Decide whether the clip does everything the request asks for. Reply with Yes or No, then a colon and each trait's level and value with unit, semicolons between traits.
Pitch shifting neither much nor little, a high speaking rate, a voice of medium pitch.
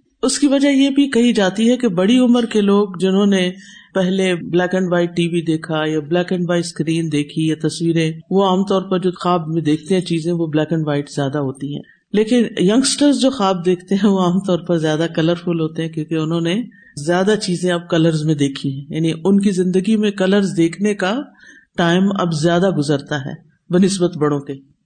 Yes: average, 3.6 semitones; fast, 210 wpm; medium, 180 Hz